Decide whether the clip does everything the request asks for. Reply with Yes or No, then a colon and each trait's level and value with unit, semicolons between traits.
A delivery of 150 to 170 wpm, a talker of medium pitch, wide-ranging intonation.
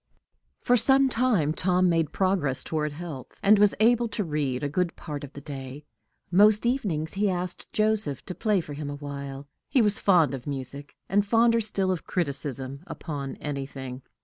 No: average, 180 wpm; medium, 165 Hz; wide, 6.4 semitones